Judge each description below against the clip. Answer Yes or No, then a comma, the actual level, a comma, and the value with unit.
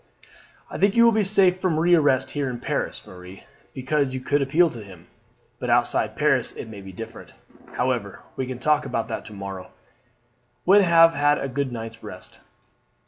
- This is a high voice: No, low, 135 Hz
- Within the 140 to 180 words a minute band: No, average, 195 wpm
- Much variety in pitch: Yes, wide, 6.6 semitones